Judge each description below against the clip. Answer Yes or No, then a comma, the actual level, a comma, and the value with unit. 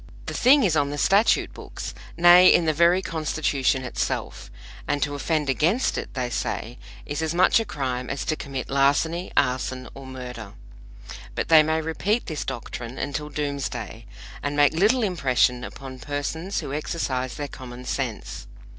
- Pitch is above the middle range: No, medium, 145 Hz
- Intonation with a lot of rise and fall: No, average, 4.0 semitones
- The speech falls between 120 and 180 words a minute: Yes, average, 165 wpm